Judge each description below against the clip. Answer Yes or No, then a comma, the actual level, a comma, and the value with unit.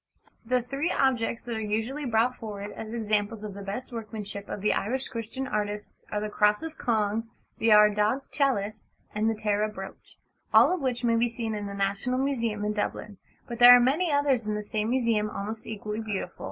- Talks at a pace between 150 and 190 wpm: No, average, 200 wpm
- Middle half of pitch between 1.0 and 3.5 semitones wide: Yes, average, 2.8 semitones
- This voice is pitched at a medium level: No, high, 220 Hz